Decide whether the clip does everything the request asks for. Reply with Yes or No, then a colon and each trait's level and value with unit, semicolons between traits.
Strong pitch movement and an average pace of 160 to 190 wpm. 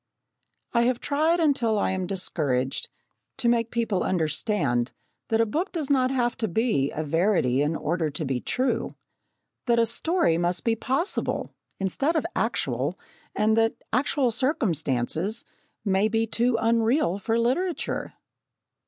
No: wide, 6.5 semitones; average, 145 wpm